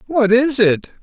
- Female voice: No, male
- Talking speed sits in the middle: Yes, average, 175 wpm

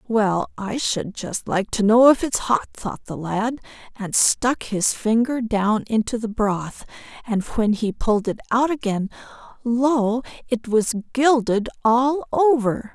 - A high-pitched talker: Yes, high, 230 Hz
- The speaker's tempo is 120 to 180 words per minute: Yes, average, 160 wpm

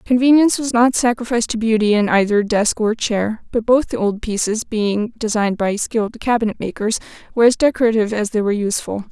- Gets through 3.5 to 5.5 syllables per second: No, 6.1 syllables/s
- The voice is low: No, high, 225 Hz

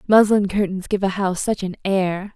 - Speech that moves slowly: No, fast, 205 wpm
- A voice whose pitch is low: No, high, 195 Hz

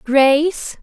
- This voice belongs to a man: No, female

